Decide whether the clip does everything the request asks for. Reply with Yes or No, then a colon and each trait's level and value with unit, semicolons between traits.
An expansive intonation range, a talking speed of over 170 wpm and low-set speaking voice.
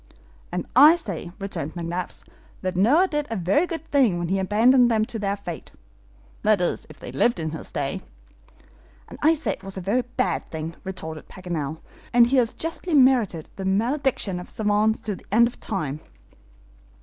No: wide, 5.9 semitones; average, 185 wpm; high, 205 Hz